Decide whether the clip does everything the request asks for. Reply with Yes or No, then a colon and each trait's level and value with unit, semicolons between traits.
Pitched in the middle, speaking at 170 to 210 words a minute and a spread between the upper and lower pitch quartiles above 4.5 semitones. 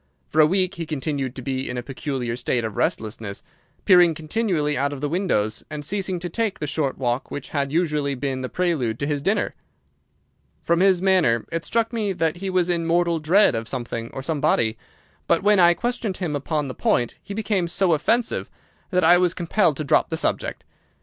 Yes: medium, 160 Hz; fast, 205 wpm; average, 5.2 semitones